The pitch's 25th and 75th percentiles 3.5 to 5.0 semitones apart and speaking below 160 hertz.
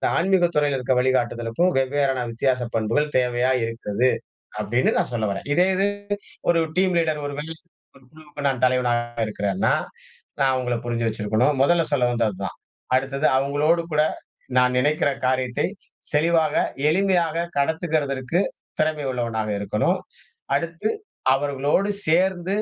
Yes: average, 4.4 semitones; low, 135 Hz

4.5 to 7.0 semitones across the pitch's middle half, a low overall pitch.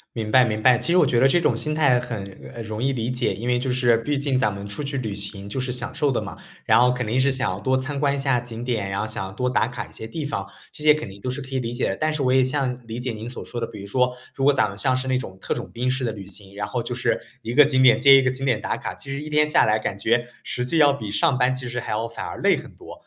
No: average, 3.1 semitones; low, 125 Hz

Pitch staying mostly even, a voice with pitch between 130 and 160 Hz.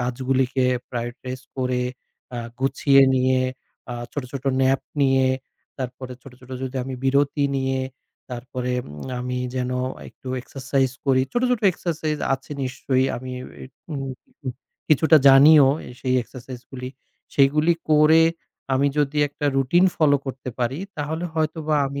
Yes: narrow, 2.3 semitones; low, 135 Hz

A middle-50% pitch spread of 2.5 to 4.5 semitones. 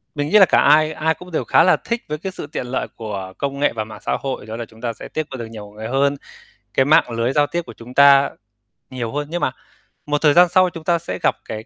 No: average, 5.3 semitones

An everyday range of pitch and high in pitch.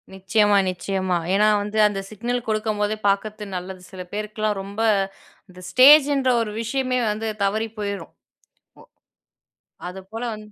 No: narrow, 2.2 semitones; high, 210 Hz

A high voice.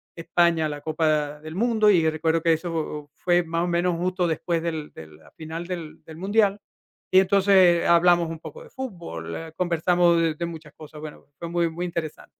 No: medium, 170 Hz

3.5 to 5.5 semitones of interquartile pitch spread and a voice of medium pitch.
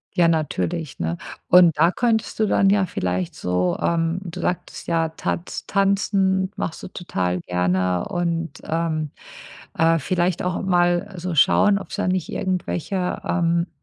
No: average, 2.8 semitones; medium, 170 Hz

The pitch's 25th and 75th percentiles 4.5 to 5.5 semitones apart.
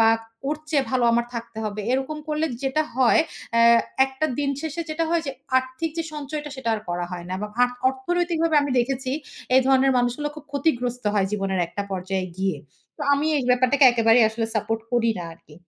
Yes: average, 4.8 semitones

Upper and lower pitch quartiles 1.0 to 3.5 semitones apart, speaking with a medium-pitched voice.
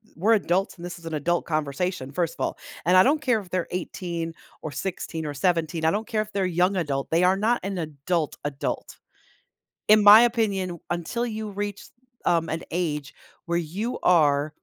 No: average, 3.9 semitones; medium, 175 Hz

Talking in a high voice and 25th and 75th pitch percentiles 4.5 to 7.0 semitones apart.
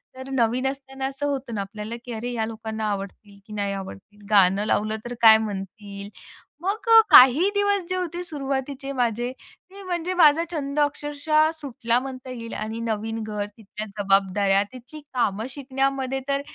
Yes: high, 245 Hz; average, 4.9 semitones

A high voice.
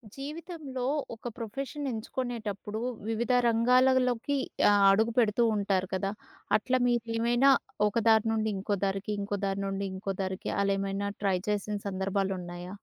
Yes: high, 215 Hz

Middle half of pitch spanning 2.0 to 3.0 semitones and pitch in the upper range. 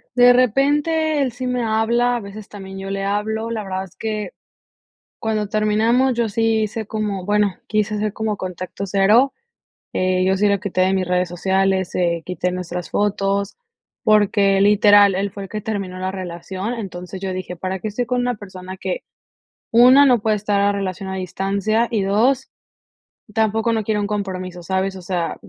Yes: average, 2.7 semitones; high, 205 Hz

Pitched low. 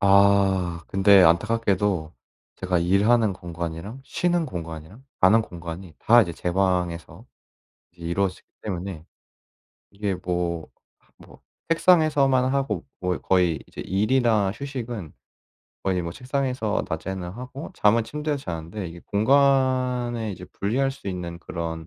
Yes: low, 100 Hz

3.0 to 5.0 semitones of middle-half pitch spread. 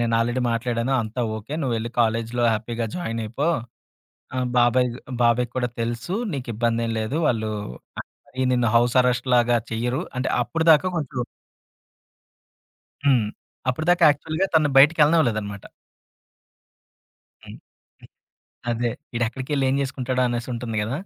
No: narrow, 2.6 semitones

